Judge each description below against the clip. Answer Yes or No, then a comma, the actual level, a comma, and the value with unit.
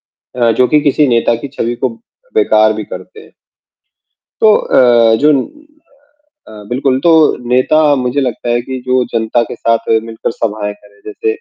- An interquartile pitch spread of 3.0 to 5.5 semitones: Yes, average, 3.3 semitones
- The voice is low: Yes, low, 125 Hz